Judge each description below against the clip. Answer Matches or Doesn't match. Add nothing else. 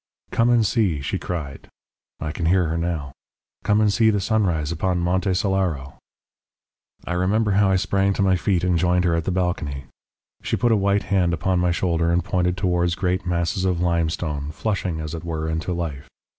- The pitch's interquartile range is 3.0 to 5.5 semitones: Doesn't match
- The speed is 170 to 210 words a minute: Matches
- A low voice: Matches